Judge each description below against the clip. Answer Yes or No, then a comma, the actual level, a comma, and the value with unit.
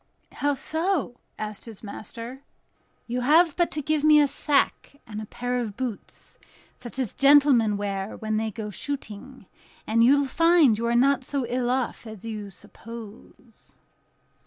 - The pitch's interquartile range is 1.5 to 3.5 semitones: No, average, 4.5 semitones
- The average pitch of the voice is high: Yes, high, 245 Hz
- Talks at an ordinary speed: Yes, average, 160 wpm